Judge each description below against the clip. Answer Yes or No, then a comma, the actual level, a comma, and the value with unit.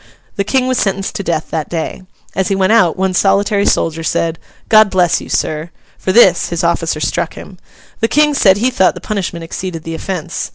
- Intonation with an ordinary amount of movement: Yes, average, 3.6 semitones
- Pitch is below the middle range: No, medium, 185 Hz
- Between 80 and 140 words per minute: No, fast, 205 wpm